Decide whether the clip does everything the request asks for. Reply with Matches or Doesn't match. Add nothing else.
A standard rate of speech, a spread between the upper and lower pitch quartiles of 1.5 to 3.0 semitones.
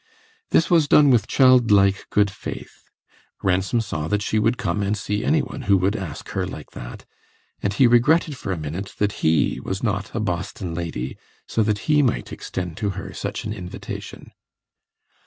Doesn't match